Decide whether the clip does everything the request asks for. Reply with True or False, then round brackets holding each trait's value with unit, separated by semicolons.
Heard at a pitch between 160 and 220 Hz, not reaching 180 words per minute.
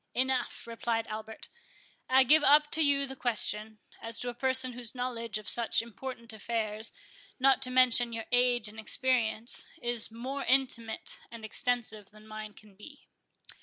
False (235 Hz; 160 wpm)